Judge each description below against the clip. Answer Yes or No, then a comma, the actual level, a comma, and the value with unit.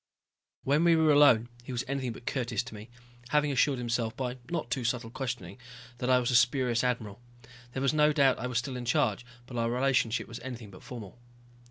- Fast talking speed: Yes, fast, 210 wpm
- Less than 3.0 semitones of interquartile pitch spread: Yes, narrow, 2.5 semitones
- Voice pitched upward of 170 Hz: No, low, 125 Hz